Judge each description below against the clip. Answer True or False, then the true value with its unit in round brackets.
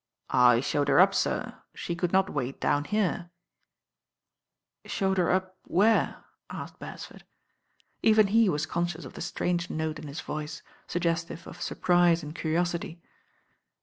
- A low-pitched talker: False (170 Hz)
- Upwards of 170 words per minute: False (155 wpm)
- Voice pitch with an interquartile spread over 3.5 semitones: False (3.2 semitones)